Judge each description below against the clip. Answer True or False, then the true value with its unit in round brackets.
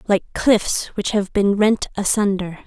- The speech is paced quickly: False (155 wpm)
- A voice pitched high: True (200 Hz)